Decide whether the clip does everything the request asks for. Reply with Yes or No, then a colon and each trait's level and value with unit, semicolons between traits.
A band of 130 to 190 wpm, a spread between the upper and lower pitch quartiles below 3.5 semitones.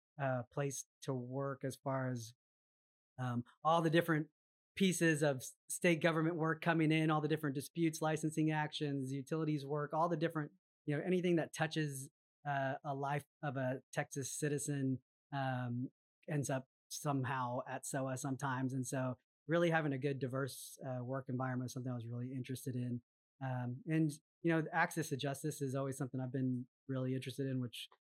Yes: average, 175 wpm; average, 3.1 semitones